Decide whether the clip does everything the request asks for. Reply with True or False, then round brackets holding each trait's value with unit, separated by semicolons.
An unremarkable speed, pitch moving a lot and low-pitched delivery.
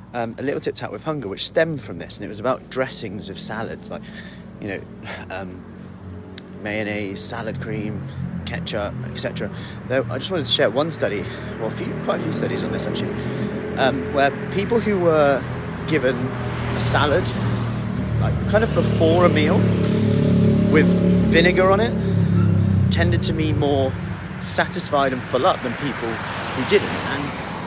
True (165 wpm; 9.0 semitones; 125 Hz)